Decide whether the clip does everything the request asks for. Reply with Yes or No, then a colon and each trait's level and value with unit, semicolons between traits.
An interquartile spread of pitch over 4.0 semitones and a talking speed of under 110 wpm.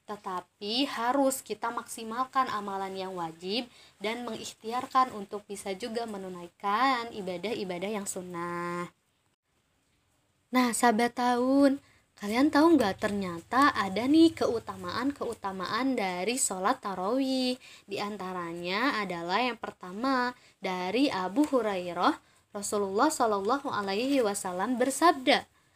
Yes: average, 4.8 semitones; average, 100 wpm